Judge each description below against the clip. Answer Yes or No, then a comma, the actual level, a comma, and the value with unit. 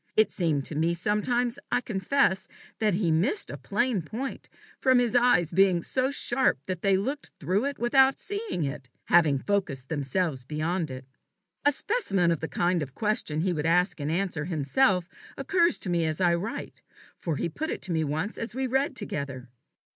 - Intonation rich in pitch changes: Yes, wide, 7.3 semitones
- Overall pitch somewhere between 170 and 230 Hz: Yes, medium, 185 Hz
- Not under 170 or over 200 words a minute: Yes, average, 185 wpm